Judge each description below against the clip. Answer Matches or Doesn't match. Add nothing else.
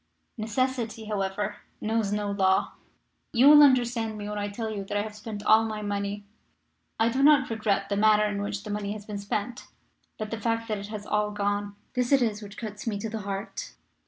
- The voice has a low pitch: Doesn't match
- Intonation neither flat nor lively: Doesn't match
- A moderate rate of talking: Doesn't match